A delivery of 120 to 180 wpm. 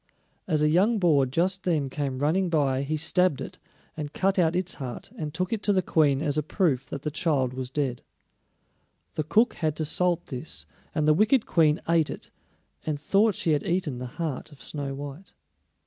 No: average, 200 wpm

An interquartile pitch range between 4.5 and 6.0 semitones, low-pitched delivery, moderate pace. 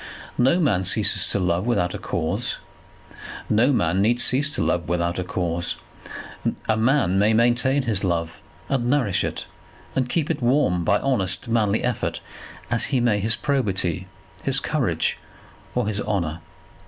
Yes: average, 5.3 semitones; low, 105 Hz; average, 155 wpm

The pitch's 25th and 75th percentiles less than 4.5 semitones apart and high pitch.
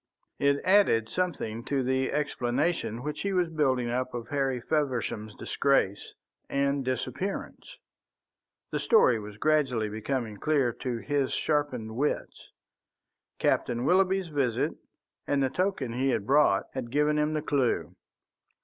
No: average, 3.9 semitones; low, 135 Hz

